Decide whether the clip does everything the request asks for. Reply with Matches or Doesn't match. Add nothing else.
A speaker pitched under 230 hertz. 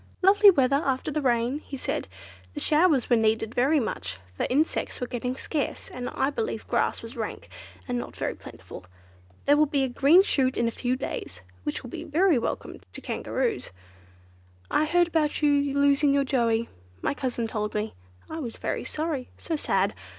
Doesn't match